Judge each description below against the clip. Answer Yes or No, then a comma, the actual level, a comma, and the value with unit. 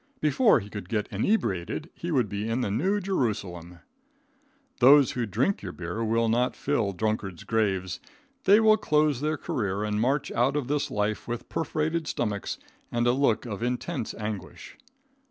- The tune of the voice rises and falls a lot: Yes, wide, 6.0 semitones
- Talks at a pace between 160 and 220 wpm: Yes, average, 165 wpm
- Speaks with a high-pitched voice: No, low, 115 Hz